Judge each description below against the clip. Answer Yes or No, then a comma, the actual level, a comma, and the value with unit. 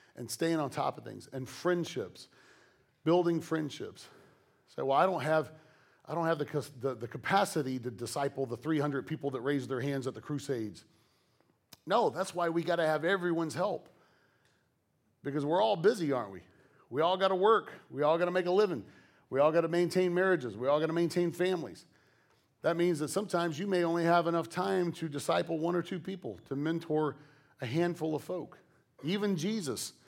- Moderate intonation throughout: Yes, average, 3.6 semitones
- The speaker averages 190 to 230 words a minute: Yes, average, 195 wpm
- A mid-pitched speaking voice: Yes, medium, 165 Hz